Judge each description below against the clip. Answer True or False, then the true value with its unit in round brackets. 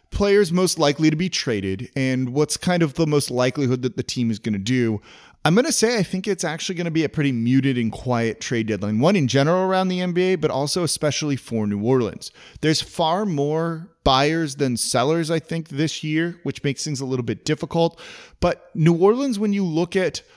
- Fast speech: True (220 wpm)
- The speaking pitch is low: False (155 Hz)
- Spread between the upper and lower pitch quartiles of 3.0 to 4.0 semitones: False (5.3 semitones)